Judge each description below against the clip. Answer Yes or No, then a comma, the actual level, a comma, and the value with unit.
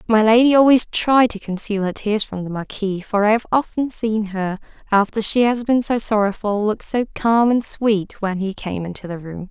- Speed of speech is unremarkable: No, fast, 215 wpm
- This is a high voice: Yes, high, 215 Hz